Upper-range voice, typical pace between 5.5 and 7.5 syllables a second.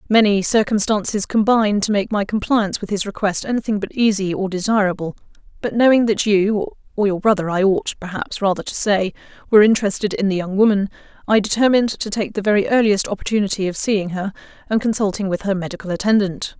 Yes: high, 205 Hz; 6.2 syllables/s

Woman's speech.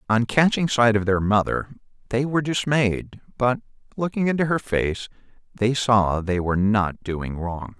No: male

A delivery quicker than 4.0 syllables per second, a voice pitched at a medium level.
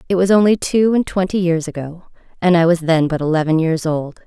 Yes: 5.6 syllables/s; medium, 170 Hz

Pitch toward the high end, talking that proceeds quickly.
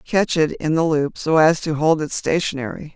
No: medium, 155 Hz; fast, 225 wpm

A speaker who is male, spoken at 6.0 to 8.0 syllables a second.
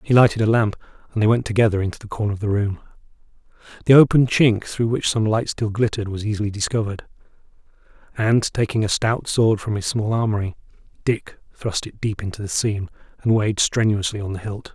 Yes: male; 6.1 syllables/s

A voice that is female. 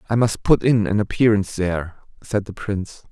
No: male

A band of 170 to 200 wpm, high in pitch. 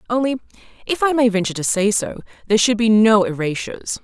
Yes: average, 195 wpm; high, 220 Hz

